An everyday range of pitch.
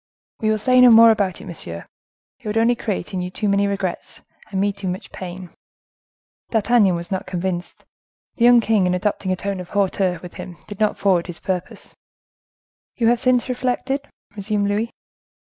Yes: average, 3.5 semitones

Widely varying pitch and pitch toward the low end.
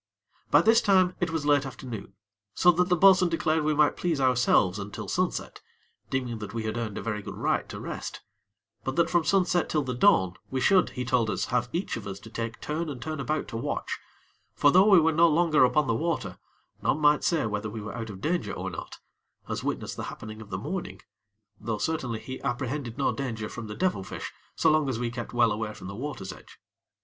Yes: wide, 6.3 semitones; low, 130 Hz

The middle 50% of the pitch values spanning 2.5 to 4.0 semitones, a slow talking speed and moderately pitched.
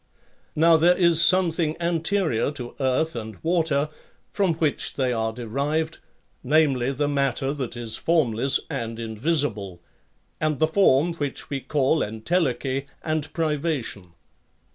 No: average, 4.6 semitones; slow, 125 wpm; medium, 145 Hz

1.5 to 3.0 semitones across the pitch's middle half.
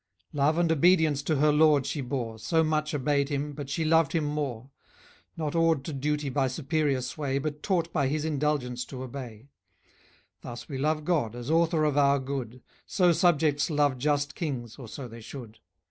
Yes: average, 2.7 semitones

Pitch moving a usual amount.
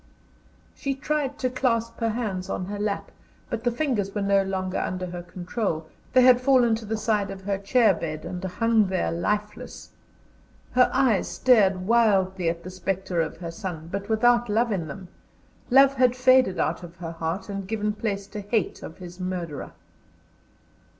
Yes: average, 4.2 semitones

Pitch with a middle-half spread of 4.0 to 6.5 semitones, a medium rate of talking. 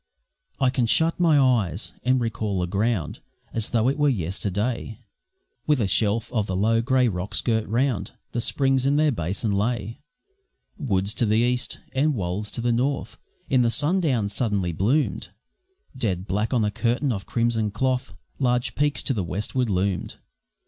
Yes: average, 4.3 semitones; average, 170 wpm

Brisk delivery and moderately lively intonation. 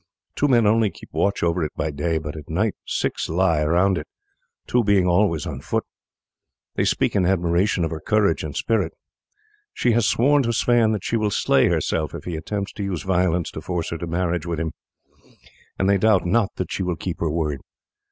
Yes: fast, 210 wpm; average, 4.1 semitones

